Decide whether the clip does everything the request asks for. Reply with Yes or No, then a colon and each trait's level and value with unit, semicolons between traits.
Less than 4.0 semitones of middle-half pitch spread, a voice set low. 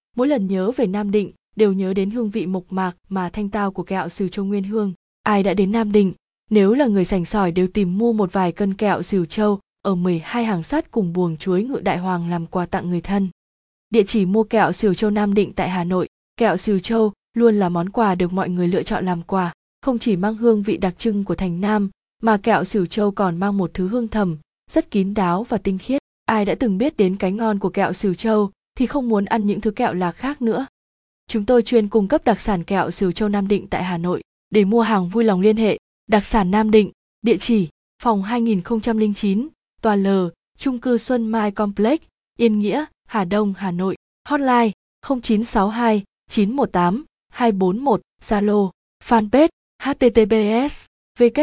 No: average, 3.1 semitones; high, 210 Hz